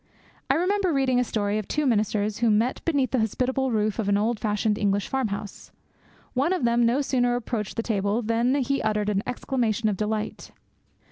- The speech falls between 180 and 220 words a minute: Yes, average, 195 wpm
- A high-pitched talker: Yes, high, 230 Hz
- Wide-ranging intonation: No, average, 3.6 semitones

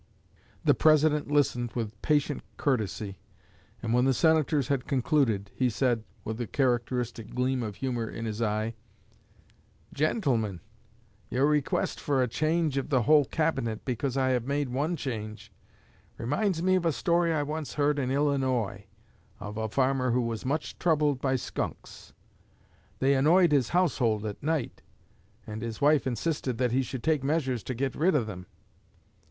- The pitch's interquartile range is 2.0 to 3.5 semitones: No, average, 4.2 semitones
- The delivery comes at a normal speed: Yes, average, 160 wpm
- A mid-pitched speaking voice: No, low, 130 Hz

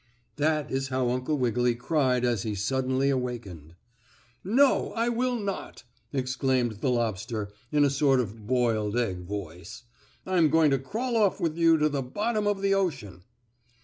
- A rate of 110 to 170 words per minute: Yes, average, 165 wpm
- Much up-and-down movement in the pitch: Yes, wide, 5.8 semitones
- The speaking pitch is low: Yes, low, 130 Hz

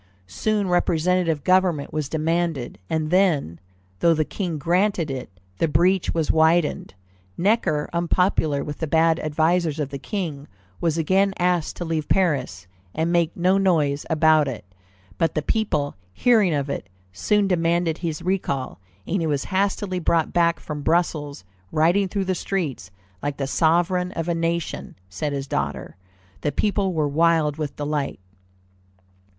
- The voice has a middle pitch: Yes, medium, 165 Hz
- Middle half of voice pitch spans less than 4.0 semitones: Yes, average, 3.5 semitones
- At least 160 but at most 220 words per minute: No, average, 150 wpm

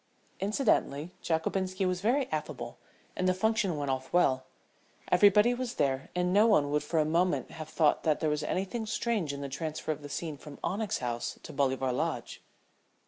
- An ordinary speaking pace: Yes, average, 185 wpm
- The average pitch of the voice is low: No, medium, 160 Hz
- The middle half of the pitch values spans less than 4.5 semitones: No, wide, 5.4 semitones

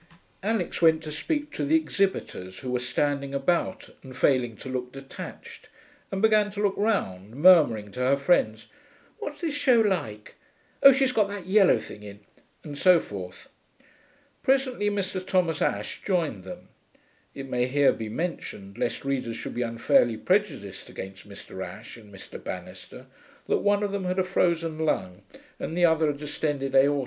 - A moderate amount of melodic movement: No, wide, 8.5 semitones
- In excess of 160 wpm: Yes, average, 170 wpm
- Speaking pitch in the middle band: Yes, medium, 150 Hz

